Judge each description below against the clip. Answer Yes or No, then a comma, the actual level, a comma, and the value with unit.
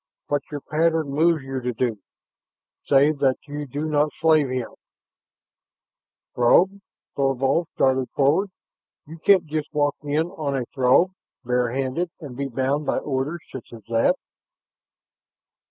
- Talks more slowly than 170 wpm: Yes, average, 140 wpm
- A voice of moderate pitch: Yes, medium, 145 Hz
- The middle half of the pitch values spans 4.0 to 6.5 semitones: No, average, 3.0 semitones